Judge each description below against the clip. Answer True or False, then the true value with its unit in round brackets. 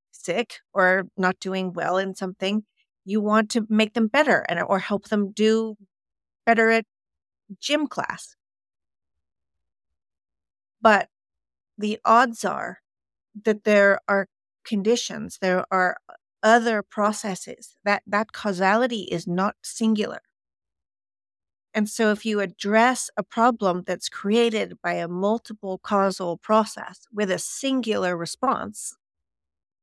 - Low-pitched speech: False (200 Hz)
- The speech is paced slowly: True (115 wpm)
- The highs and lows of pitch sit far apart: False (3.8 semitones)